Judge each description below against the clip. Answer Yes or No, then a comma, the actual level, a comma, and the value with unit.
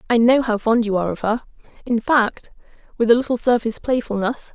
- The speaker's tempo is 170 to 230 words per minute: Yes, average, 200 wpm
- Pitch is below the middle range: No, high, 230 Hz